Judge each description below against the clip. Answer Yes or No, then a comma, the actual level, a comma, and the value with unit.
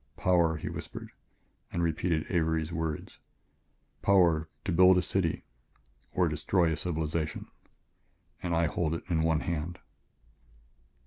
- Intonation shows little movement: Yes, narrow, 1.7 semitones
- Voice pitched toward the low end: Yes, very low, 80 Hz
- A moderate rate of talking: No, slow, 125 wpm